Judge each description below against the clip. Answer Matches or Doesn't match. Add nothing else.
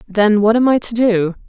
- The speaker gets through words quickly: Matches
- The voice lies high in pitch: Matches